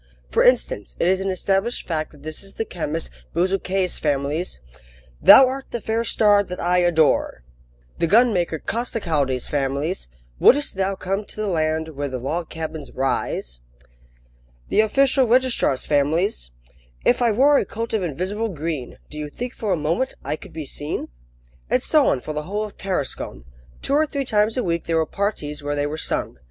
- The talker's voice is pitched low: No, medium, 175 Hz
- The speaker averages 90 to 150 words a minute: No, average, 180 wpm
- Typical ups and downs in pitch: No, wide, 6.1 semitones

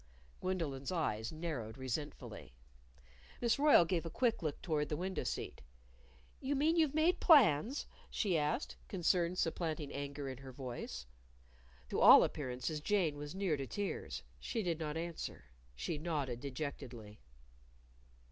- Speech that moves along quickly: No, average, 140 wpm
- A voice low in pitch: No, medium, 155 Hz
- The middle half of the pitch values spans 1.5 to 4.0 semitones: No, average, 5.2 semitones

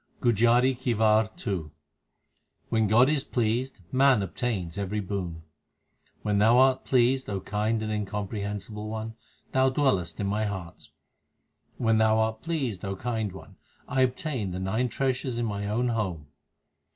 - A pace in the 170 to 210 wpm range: No, average, 150 wpm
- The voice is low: Yes, low, 110 Hz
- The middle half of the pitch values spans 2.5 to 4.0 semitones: Yes, average, 3.6 semitones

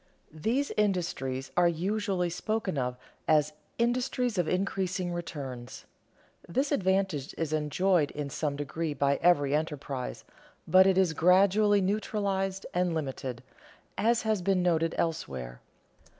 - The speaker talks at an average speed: No, slow, 125 wpm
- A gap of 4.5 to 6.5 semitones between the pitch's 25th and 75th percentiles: Yes, average, 4.9 semitones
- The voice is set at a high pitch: No, medium, 175 Hz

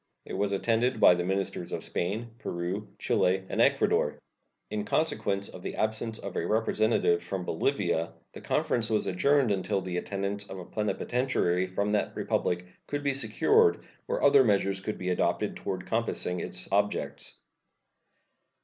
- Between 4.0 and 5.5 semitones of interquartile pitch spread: No, average, 3.4 semitones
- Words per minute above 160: No, average, 155 wpm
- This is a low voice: Yes, low, 100 Hz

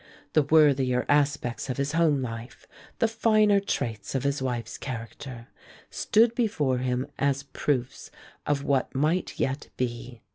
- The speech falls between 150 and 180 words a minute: No, average, 140 wpm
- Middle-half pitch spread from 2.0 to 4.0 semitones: Yes, average, 3.4 semitones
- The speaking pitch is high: No, medium, 140 Hz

